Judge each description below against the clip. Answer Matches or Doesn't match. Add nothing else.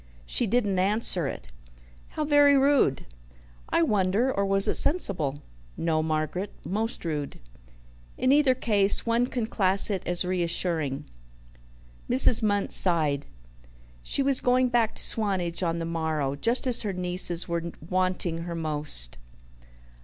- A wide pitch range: Matches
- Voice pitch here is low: Doesn't match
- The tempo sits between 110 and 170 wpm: Matches